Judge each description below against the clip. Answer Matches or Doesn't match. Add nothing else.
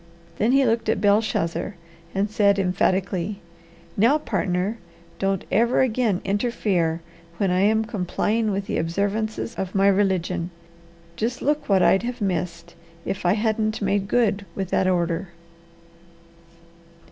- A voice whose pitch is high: Matches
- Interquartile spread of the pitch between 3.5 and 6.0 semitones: Doesn't match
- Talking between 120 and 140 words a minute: Matches